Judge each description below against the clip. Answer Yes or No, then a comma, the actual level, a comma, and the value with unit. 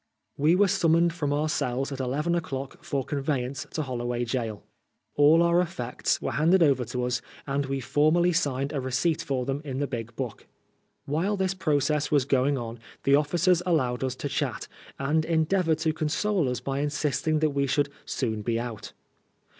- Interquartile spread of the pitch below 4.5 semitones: Yes, average, 3.6 semitones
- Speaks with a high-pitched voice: No, medium, 145 Hz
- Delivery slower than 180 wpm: No, average, 185 wpm